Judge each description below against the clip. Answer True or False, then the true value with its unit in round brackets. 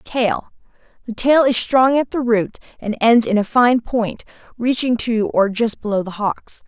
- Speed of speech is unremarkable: True (180 wpm)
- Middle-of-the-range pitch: False (210 Hz)